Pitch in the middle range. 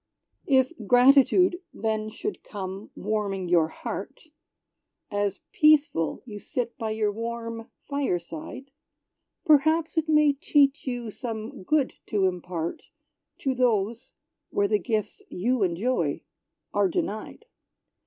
No: high, 230 Hz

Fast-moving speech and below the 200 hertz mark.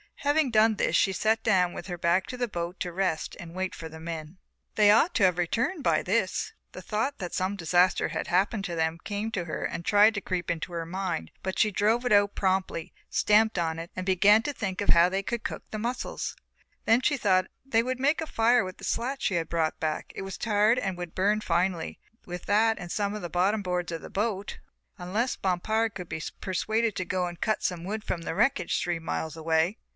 Yes: fast, 225 wpm; high, 190 Hz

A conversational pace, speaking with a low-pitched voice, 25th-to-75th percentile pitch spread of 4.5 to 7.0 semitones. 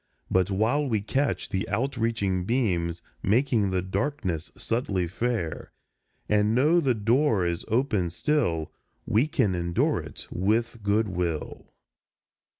No: slow, 125 wpm; low, 105 Hz; average, 5.2 semitones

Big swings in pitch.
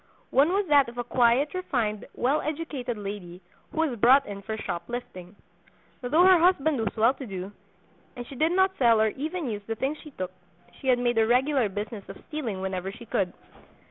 Yes: wide, 5.8 semitones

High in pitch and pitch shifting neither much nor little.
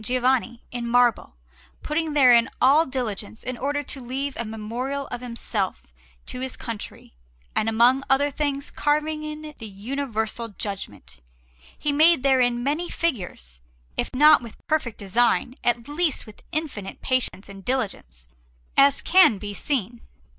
Yes: very high, 250 Hz; average, 4.3 semitones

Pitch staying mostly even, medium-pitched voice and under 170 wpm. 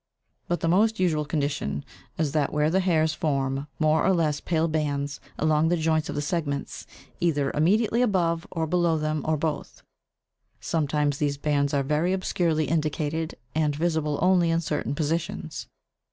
Yes: narrow, 2.3 semitones; medium, 155 Hz; average, 160 wpm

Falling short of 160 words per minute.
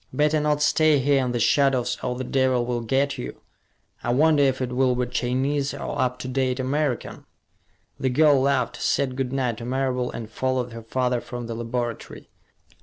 No: average, 185 wpm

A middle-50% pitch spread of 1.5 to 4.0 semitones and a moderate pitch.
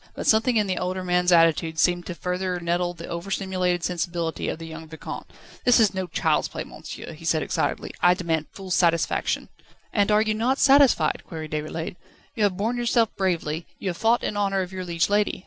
Yes: average, 3.3 semitones; medium, 180 Hz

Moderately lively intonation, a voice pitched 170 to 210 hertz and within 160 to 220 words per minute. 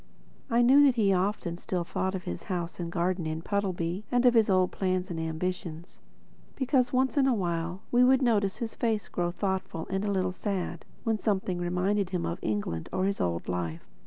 Yes: average, 3.8 semitones; medium, 185 Hz; average, 200 wpm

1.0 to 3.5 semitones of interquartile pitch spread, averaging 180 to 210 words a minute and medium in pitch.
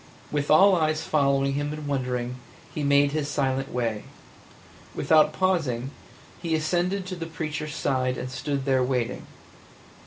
No: average, 3.0 semitones; average, 145 wpm; medium, 145 Hz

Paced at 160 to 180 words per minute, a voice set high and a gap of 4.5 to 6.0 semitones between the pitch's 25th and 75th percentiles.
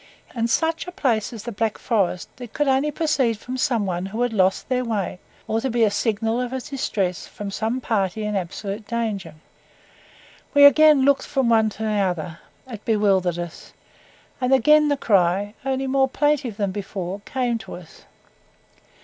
Yes: average, 175 wpm; high, 225 Hz; average, 4.8 semitones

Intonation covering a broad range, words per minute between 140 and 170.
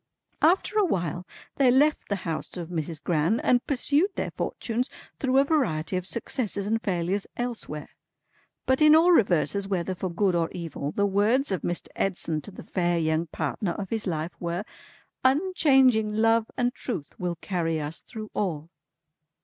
Yes: wide, 6.4 semitones; average, 165 wpm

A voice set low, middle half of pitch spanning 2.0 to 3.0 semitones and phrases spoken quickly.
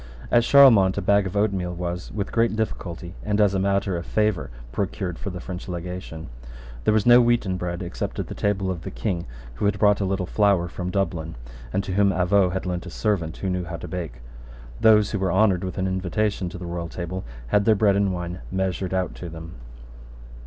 Yes: very low, 95 Hz; narrow, 2.5 semitones; fast, 215 wpm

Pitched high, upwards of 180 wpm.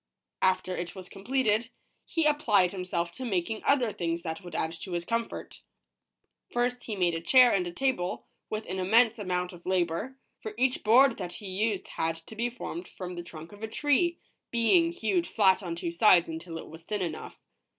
Yes: high, 195 Hz; average, 195 wpm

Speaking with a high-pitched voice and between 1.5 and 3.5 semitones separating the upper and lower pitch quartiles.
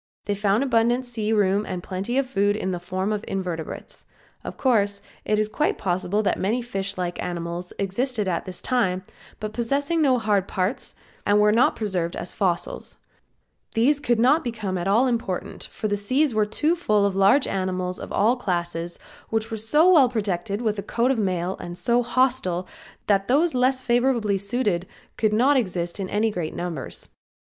No: high, 210 Hz; average, 4.6 semitones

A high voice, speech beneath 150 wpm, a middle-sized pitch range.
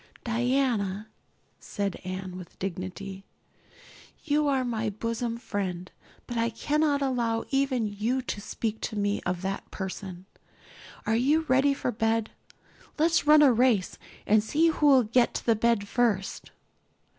Yes: high, 230 Hz; average, 140 wpm; average, 4.4 semitones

